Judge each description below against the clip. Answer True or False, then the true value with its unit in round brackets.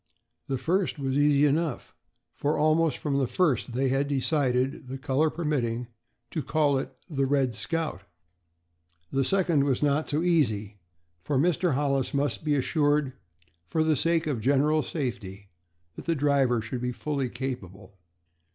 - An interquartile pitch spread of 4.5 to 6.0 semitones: False (3.2 semitones)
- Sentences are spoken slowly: False (155 wpm)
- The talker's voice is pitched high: False (140 Hz)